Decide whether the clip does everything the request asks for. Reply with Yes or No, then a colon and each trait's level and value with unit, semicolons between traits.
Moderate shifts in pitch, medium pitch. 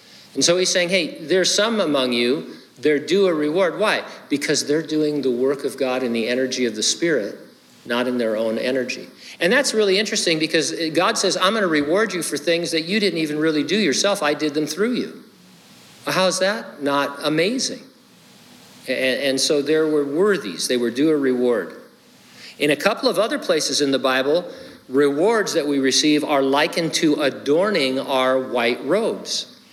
No: wide, 6.1 semitones; medium, 150 Hz